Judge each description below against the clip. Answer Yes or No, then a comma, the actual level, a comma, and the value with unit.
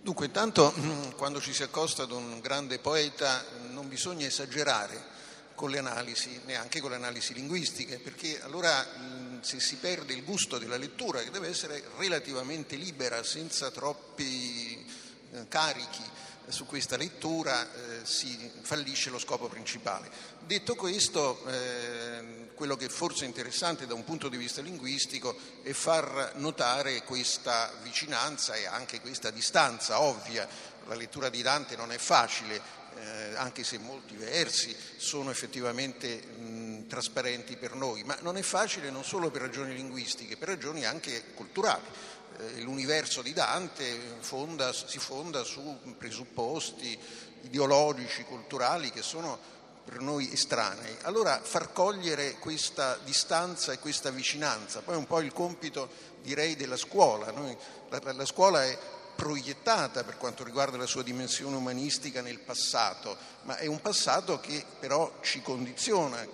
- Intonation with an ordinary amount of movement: Yes, average, 3.5 semitones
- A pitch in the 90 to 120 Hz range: No, low, 135 Hz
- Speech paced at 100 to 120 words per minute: No, average, 140 wpm